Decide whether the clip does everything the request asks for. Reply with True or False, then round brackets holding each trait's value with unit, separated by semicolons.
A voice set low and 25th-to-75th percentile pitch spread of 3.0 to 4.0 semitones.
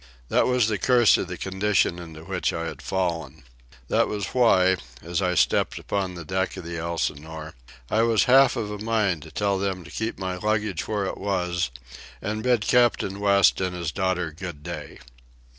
True (95 Hz; 3.6 semitones)